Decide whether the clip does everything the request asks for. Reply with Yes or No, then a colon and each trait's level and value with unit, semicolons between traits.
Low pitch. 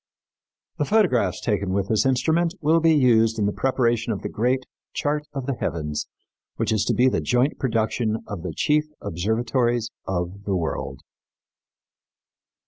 Yes: low, 115 Hz